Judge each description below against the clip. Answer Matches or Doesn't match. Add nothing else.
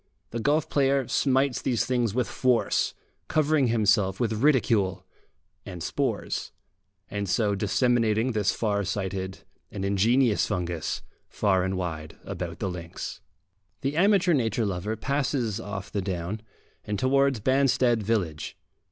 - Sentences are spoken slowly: Matches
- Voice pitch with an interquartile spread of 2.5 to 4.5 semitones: Doesn't match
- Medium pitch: Doesn't match